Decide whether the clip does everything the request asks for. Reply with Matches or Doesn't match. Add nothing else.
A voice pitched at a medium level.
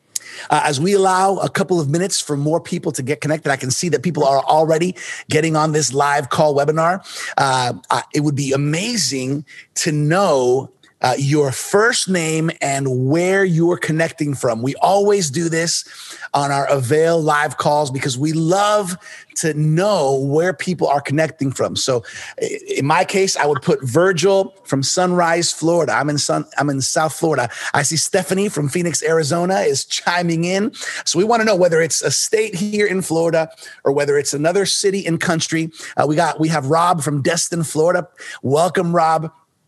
Matches